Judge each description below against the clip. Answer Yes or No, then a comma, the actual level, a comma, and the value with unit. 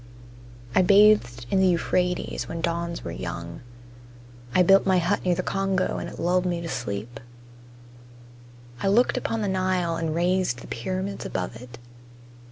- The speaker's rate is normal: Yes, average, 160 wpm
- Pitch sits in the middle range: Yes, medium, 180 Hz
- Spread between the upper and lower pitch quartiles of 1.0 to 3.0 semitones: Yes, narrow, 2.5 semitones